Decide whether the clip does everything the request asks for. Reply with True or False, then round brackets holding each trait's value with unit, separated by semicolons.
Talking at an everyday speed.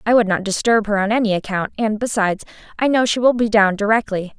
False (230 wpm)